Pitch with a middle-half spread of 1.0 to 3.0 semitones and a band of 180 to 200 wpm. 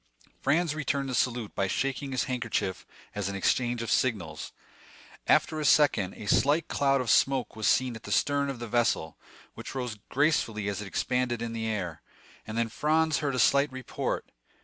No: average, 4.2 semitones; average, 185 wpm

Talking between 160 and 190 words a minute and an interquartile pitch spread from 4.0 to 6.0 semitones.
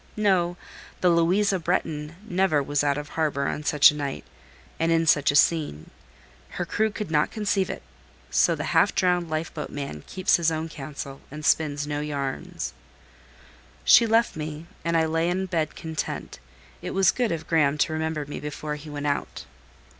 No: average, 180 wpm; average, 2.9 semitones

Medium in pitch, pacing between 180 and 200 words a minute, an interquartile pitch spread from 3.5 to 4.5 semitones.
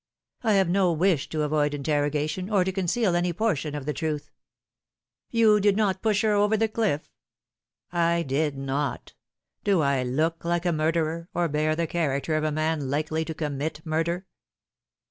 Yes: medium, 160 Hz; average, 185 wpm; average, 3.8 semitones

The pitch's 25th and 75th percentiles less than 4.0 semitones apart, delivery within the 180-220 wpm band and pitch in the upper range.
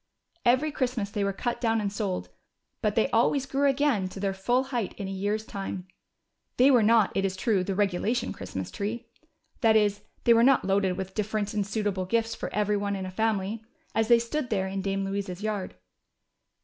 Yes: average, 3.1 semitones; average, 200 wpm; high, 210 Hz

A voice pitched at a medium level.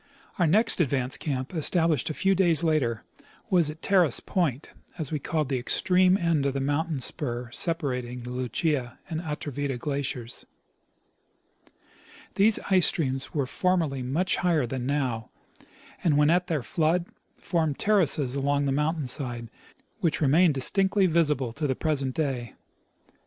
Yes: medium, 150 Hz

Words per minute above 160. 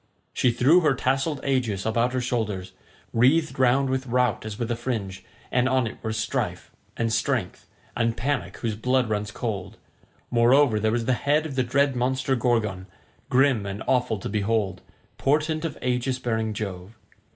Yes: average, 170 wpm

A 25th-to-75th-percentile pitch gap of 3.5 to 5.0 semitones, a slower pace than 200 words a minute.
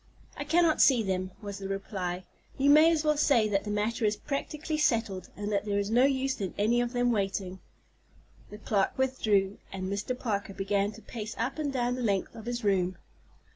No: average, 4.7 semitones; fast, 205 wpm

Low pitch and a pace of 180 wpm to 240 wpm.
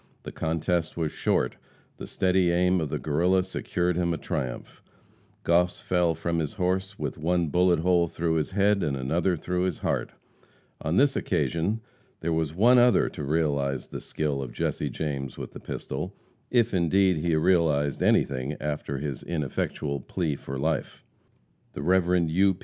No: very low, 85 Hz; average, 165 wpm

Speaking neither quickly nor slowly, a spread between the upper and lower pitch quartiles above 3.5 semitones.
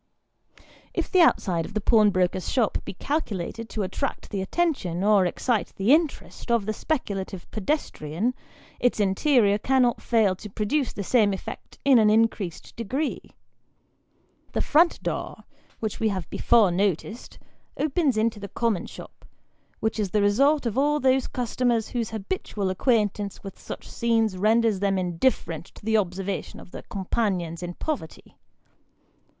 Yes: average, 150 wpm; average, 4.3 semitones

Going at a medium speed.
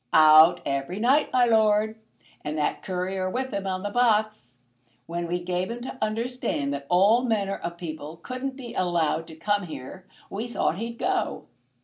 Yes: average, 170 wpm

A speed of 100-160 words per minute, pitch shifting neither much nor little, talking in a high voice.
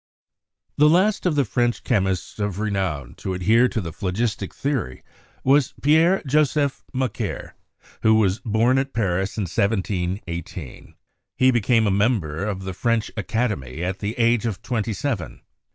No: average, 150 wpm; average, 5.0 semitones; low, 110 Hz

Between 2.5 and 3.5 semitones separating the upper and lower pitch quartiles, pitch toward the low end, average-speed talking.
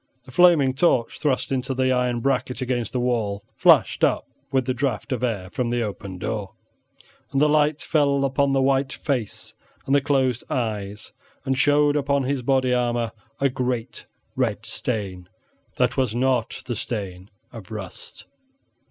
Yes: average, 3.0 semitones; low, 125 Hz; average, 160 wpm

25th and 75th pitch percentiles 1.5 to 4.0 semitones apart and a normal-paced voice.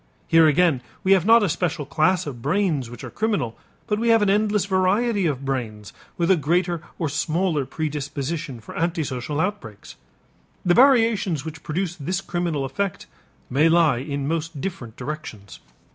No: average, 5.1 semitones; average, 160 wpm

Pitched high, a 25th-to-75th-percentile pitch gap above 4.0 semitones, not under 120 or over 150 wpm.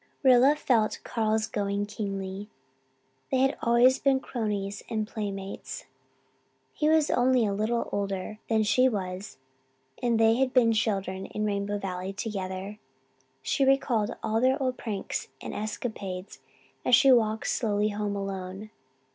No: high, 215 Hz; average, 3.4 semitones; average, 140 wpm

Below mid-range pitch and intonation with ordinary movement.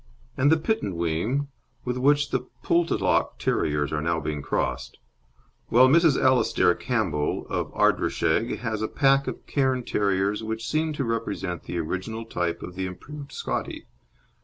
No: low, 115 Hz; wide, 7.6 semitones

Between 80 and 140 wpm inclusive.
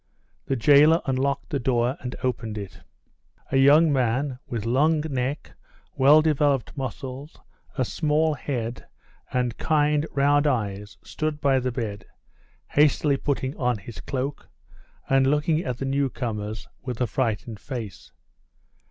Yes: slow, 135 wpm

